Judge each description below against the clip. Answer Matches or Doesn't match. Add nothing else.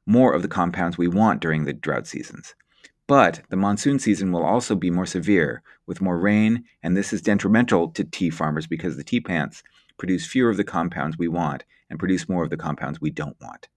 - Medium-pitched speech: Doesn't match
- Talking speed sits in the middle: Doesn't match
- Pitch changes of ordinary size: Matches